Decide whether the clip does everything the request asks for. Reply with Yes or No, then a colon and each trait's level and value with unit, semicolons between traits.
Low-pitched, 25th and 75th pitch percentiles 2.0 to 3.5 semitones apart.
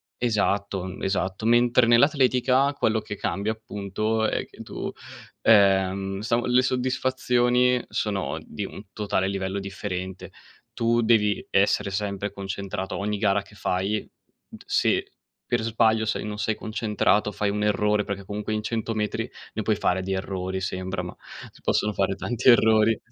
Yes: low, 105 Hz; narrow, 2.6 semitones